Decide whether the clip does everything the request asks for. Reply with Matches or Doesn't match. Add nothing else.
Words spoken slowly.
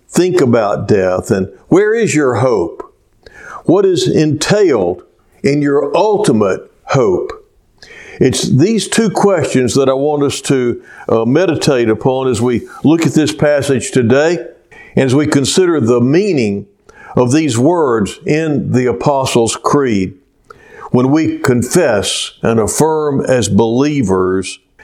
Matches